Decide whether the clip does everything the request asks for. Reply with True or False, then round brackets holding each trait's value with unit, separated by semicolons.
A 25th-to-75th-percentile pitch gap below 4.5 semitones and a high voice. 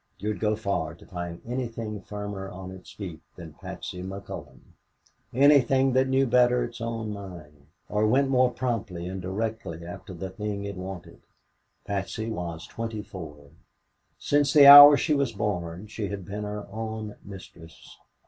False (4.1 semitones; 105 Hz)